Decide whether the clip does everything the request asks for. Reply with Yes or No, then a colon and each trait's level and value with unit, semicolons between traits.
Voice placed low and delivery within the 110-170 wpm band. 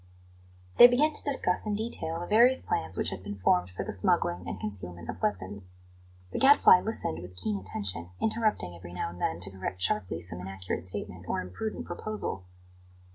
No: very low, 95 Hz; average, 185 wpm